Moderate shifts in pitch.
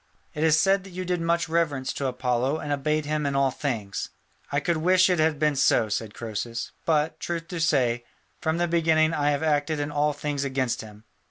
Yes: average, 3.4 semitones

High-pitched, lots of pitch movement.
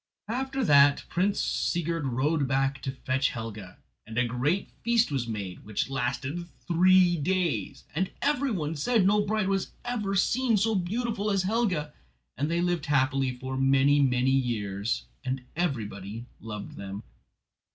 No: medium, 145 Hz; wide, 7.0 semitones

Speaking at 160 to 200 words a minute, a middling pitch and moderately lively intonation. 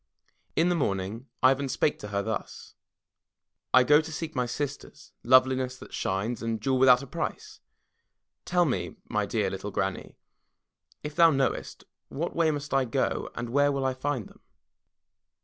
No: average, 165 wpm; low, 130 Hz; average, 3.2 semitones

